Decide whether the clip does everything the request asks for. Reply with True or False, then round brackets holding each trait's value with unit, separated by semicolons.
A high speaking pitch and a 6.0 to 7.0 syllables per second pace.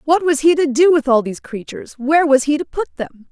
True (290 Hz; 6.3 syllables/s)